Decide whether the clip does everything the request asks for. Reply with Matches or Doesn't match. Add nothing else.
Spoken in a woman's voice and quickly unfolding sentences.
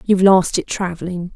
Doesn't match